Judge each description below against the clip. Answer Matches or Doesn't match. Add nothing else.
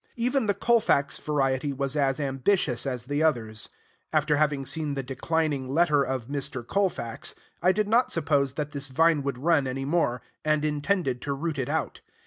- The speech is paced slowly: Doesn't match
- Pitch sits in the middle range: Matches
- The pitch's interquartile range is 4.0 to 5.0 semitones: Doesn't match